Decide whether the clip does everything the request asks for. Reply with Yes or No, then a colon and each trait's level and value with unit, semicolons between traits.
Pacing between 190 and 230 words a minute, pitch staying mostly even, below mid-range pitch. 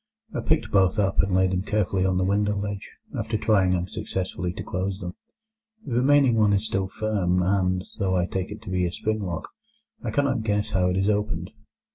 Yes: fast, 205 wpm; narrow, 2.2 semitones; very low, 95 Hz